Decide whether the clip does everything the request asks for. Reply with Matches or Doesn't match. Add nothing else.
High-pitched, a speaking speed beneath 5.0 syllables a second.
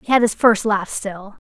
Matches